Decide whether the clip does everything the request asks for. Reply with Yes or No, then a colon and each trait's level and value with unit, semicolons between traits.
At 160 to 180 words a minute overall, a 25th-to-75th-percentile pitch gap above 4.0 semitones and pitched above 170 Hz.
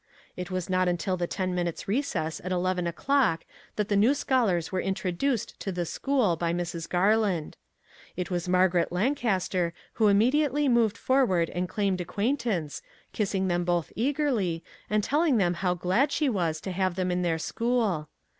Yes: average, 175 wpm; average, 4.6 semitones; medium, 185 Hz